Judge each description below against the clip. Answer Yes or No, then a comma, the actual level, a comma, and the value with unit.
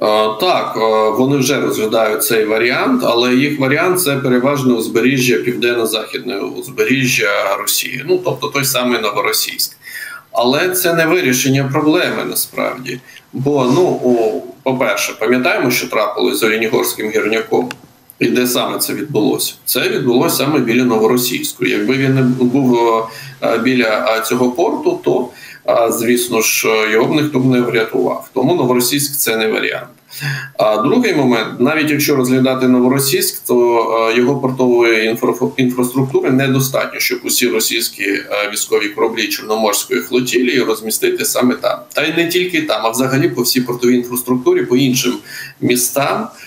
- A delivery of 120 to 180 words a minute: Yes, average, 135 wpm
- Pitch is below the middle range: Yes, low, 125 Hz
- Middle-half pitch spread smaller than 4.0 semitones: Yes, average, 2.9 semitones